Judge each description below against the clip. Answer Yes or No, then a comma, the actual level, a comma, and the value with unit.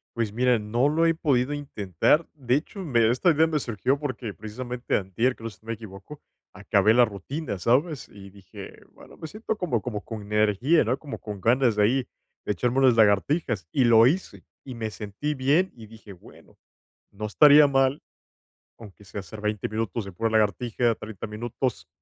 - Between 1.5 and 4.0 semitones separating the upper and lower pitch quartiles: No, average, 4.6 semitones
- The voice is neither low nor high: No, low, 115 Hz